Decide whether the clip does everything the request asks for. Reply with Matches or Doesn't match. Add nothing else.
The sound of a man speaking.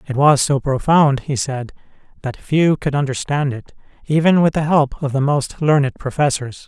Matches